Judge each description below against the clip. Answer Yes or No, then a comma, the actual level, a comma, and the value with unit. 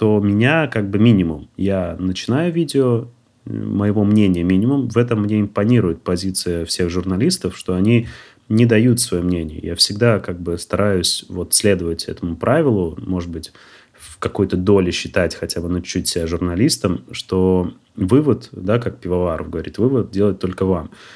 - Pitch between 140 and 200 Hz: No, very low, 95 Hz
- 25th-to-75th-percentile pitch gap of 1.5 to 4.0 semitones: No, average, 4.7 semitones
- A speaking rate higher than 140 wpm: Yes, fast, 160 wpm